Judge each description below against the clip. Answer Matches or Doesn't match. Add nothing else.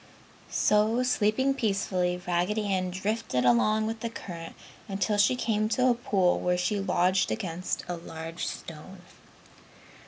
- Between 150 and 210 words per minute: Doesn't match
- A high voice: Matches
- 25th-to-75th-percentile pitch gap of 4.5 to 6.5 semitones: Doesn't match